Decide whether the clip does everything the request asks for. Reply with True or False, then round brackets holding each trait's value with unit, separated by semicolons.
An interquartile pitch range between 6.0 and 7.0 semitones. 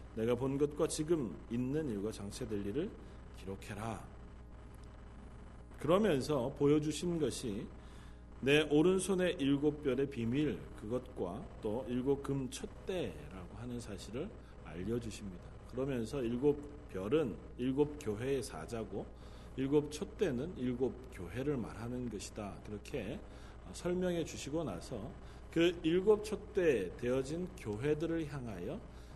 True (6.5 semitones)